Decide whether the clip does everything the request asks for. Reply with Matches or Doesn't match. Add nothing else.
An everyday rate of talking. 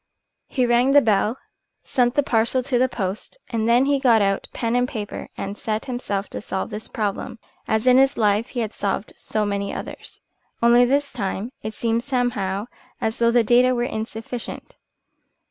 Matches